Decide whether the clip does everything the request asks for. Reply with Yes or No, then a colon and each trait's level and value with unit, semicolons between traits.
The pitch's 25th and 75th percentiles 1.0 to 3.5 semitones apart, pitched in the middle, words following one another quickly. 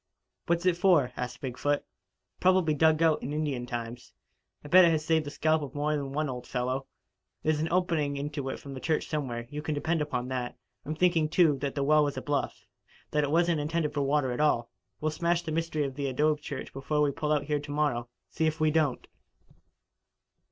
Yes: narrow, 2.4 semitones; medium, 150 Hz; fast, 220 wpm